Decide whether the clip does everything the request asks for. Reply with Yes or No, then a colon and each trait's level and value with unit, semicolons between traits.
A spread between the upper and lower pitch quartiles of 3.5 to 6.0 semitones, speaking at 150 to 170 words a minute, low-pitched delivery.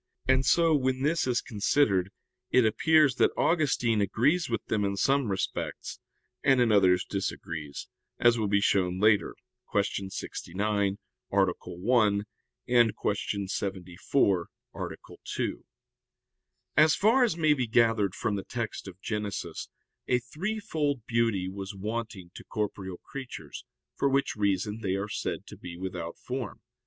No: average, 5.0 semitones; average, 140 wpm; low, 110 Hz